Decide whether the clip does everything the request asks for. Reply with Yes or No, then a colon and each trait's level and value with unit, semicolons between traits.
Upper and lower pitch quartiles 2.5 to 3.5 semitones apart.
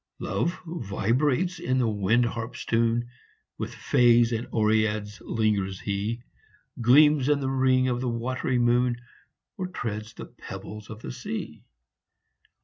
Yes: average, 2.9 semitones